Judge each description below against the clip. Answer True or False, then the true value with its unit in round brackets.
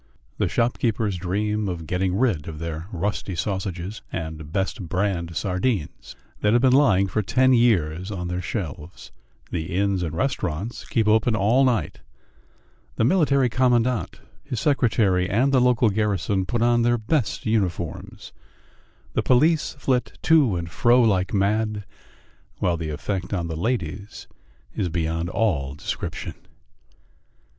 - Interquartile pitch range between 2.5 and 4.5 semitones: False (5.2 semitones)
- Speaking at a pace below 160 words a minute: True (140 wpm)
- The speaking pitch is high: False (100 Hz)